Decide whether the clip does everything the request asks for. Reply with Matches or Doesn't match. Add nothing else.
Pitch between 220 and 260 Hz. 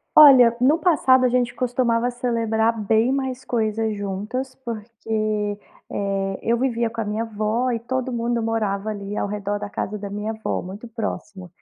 Matches